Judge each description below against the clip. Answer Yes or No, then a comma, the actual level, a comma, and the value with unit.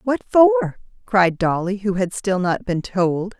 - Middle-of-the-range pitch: No, high, 195 Hz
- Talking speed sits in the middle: Yes, average, 175 wpm